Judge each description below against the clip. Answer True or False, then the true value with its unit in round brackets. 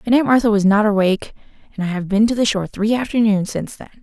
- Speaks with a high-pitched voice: True (215 Hz)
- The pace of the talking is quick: True (240 wpm)